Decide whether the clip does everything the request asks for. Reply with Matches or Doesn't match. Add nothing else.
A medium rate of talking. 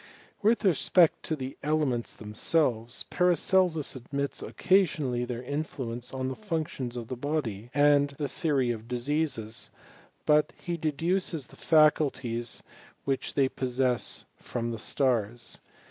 Doesn't match